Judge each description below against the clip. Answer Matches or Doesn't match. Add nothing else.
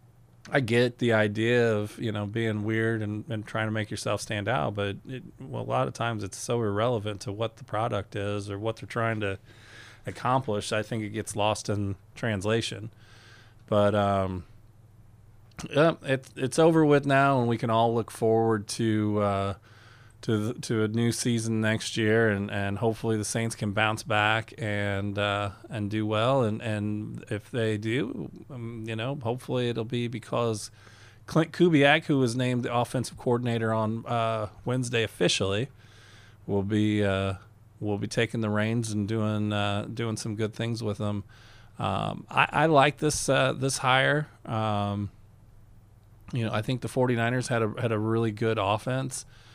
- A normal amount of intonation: Doesn't match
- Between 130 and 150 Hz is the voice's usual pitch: Doesn't match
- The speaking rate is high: Doesn't match